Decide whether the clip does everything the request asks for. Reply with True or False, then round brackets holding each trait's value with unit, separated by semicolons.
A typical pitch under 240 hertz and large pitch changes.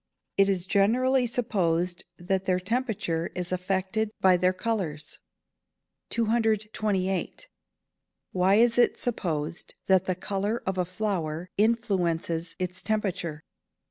False (190 Hz; 3.6 semitones)